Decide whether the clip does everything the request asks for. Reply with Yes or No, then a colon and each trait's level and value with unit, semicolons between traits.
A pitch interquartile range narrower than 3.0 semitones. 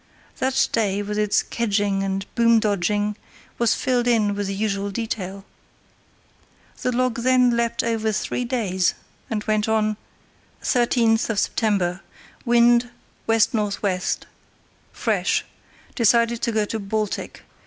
Yes: narrow, 2.5 semitones